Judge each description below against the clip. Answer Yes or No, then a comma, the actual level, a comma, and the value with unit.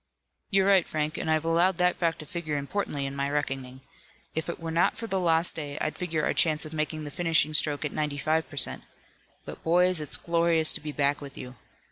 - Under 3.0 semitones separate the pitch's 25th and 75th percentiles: Yes, narrow, 2.5 semitones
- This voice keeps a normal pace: No, fast, 225 wpm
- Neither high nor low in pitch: Yes, medium, 155 Hz